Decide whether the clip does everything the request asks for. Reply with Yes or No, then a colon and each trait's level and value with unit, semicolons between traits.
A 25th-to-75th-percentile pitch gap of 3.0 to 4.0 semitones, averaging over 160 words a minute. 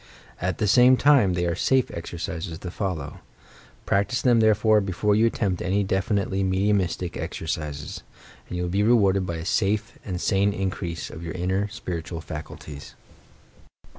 No: average, 3.3 semitones; average, 155 wpm